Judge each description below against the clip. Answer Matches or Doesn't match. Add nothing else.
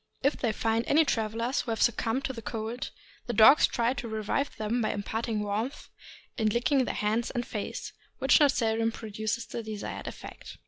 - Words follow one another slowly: Doesn't match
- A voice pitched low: Doesn't match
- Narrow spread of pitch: Matches